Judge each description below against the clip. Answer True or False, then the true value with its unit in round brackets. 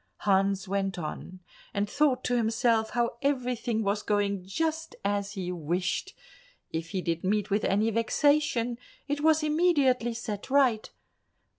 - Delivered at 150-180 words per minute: False (140 wpm)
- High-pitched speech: True (220 Hz)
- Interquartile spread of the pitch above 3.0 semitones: True (4.9 semitones)